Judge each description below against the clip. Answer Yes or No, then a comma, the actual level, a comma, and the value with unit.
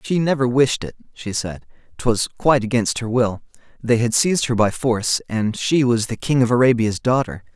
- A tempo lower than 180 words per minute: No, average, 200 wpm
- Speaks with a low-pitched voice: Yes, low, 120 Hz